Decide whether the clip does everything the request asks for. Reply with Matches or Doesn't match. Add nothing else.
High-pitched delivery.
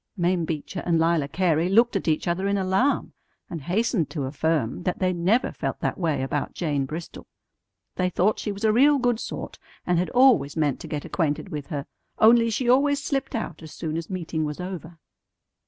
Doesn't match